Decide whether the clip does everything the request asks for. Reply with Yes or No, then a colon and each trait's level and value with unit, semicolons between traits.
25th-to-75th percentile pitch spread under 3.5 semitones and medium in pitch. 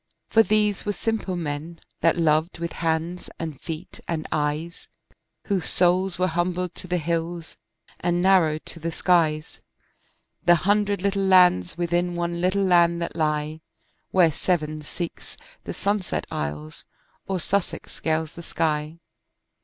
Yes: narrow, 2.5 semitones; medium, 170 Hz